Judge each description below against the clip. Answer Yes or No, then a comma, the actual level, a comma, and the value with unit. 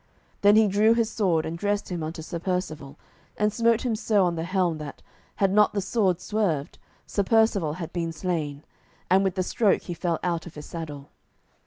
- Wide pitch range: No, average, 4.2 semitones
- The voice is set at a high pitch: No, medium, 180 Hz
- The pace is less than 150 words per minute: No, average, 200 wpm